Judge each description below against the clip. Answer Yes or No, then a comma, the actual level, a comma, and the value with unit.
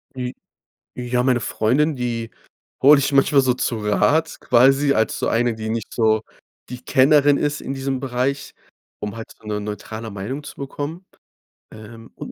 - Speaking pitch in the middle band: No, low, 125 Hz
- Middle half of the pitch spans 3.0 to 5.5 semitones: Yes, average, 3.7 semitones